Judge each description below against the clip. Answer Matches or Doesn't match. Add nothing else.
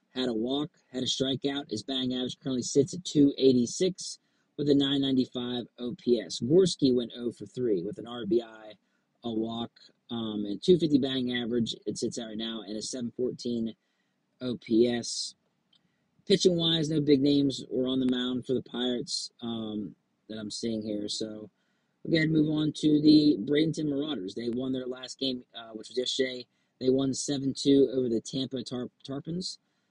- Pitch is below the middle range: Matches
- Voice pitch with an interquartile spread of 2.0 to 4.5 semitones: Matches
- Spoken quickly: Doesn't match